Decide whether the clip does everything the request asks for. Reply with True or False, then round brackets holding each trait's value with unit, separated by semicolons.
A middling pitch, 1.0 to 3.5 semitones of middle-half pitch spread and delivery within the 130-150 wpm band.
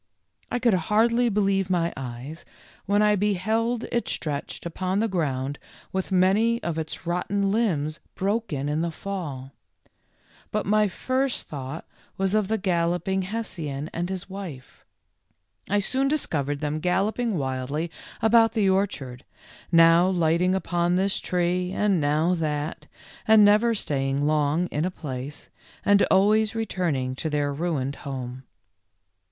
False (180 Hz; 5.5 semitones; 140 wpm)